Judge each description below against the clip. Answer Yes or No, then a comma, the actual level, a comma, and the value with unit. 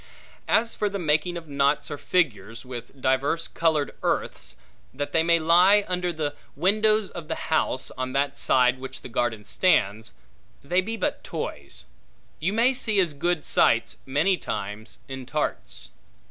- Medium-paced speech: Yes, average, 160 wpm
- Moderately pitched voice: Yes, medium, 155 Hz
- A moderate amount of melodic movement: No, wide, 5.8 semitones